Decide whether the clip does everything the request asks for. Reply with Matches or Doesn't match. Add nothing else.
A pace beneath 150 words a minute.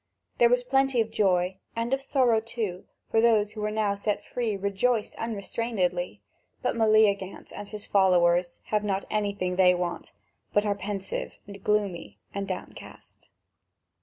Matches